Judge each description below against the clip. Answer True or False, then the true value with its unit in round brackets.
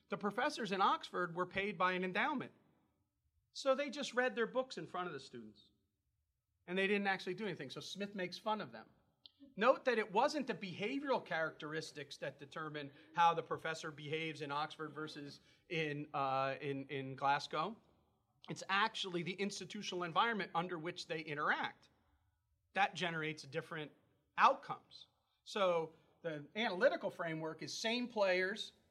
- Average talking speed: True (150 wpm)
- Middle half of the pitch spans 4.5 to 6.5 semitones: True (5.0 semitones)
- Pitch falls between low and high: True (170 Hz)